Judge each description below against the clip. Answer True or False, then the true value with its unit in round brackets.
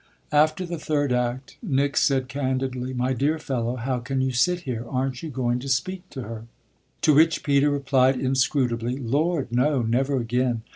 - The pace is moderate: True (175 wpm)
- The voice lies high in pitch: False (130 Hz)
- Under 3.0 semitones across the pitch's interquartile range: True (2.5 semitones)